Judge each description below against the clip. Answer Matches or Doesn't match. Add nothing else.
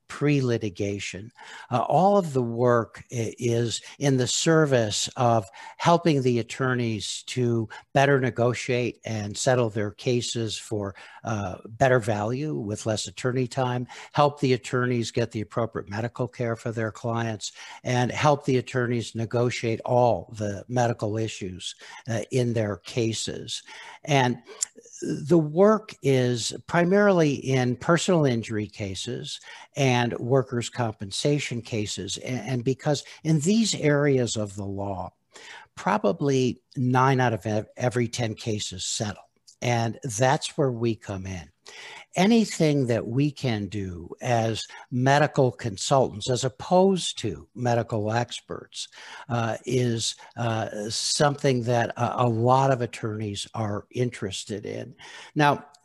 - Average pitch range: Matches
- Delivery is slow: Matches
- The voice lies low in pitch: Matches